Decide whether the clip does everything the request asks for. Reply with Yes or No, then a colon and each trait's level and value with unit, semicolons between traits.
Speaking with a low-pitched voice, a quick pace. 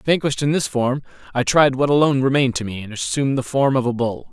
Yes: low, 130 Hz; fast, 250 wpm